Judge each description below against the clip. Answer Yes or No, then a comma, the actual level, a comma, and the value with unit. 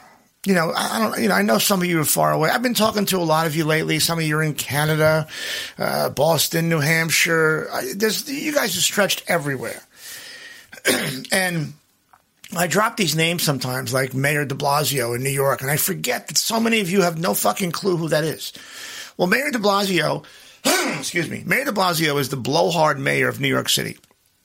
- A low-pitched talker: No, medium, 165 Hz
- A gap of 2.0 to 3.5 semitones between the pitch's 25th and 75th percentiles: No, average, 5.0 semitones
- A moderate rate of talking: No, fast, 210 wpm